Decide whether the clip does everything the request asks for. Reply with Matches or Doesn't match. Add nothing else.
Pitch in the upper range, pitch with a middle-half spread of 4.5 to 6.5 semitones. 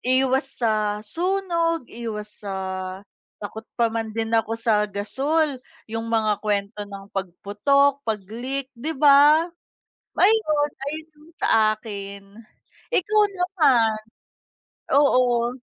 Matches